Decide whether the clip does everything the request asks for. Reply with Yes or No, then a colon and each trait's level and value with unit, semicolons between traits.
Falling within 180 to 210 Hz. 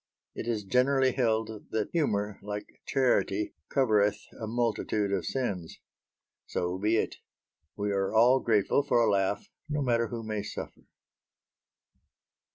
No: low, 110 Hz